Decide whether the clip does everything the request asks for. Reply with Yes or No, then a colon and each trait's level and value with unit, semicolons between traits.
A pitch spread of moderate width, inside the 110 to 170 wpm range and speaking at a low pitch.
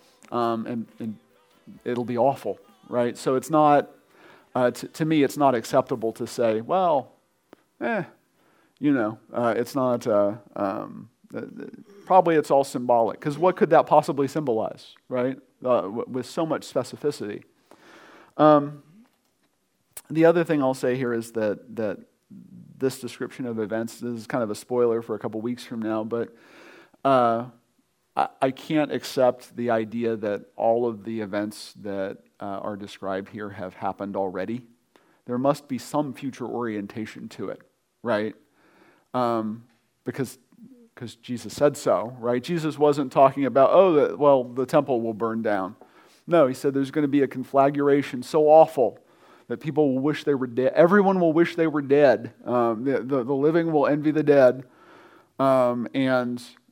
Yes: average, 4.1 semitones; average, 165 wpm; low, 125 Hz